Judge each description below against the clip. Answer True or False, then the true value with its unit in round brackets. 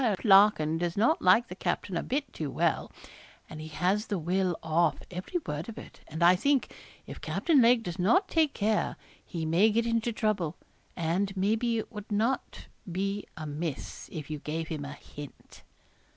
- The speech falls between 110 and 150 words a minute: False (180 wpm)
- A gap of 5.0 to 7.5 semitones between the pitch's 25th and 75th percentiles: True (5.4 semitones)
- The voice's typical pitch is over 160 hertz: True (190 Hz)